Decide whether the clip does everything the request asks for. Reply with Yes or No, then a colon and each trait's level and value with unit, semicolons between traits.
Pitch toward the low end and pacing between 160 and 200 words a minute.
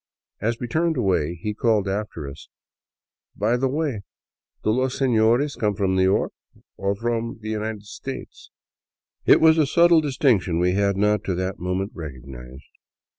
Yes: low, 105 Hz; average, 170 wpm